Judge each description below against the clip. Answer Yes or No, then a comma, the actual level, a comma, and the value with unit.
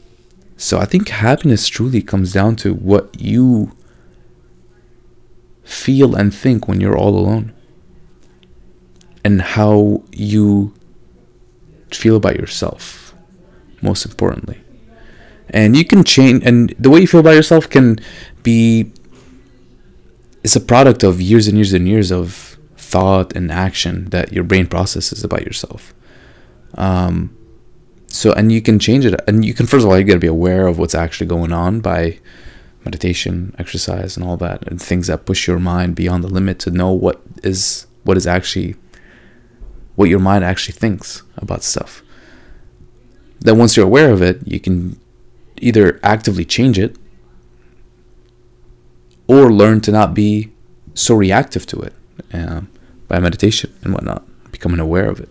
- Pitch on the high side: No, very low, 95 Hz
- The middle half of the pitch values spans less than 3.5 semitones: No, average, 4.0 semitones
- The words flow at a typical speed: Yes, average, 150 wpm